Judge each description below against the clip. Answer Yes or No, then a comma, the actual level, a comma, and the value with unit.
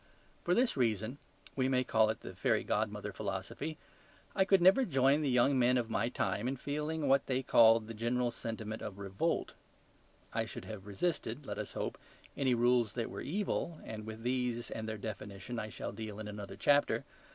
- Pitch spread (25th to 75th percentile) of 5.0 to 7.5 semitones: No, average, 3.7 semitones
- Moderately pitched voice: No, low, 120 Hz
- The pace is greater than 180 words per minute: Yes, average, 190 wpm